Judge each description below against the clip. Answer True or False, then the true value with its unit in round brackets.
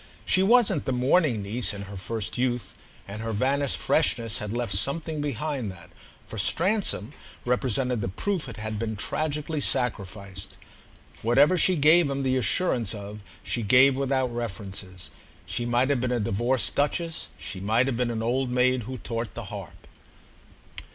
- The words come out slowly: False (160 wpm)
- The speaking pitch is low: True (125 Hz)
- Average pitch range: True (4.5 semitones)